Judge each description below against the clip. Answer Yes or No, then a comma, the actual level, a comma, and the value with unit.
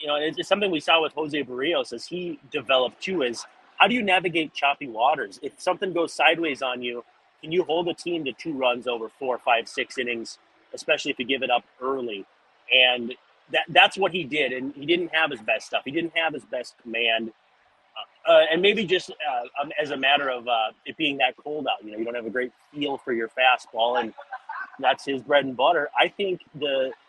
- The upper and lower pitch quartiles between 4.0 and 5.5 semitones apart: Yes, average, 5.2 semitones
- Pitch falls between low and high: Yes, medium, 145 Hz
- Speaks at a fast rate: Yes, fast, 220 wpm